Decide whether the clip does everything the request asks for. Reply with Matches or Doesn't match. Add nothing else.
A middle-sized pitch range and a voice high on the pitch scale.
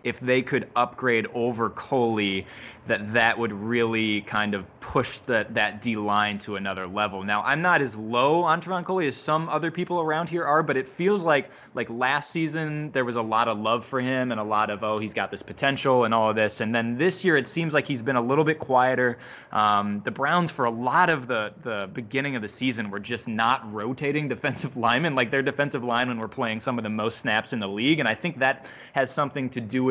Doesn't match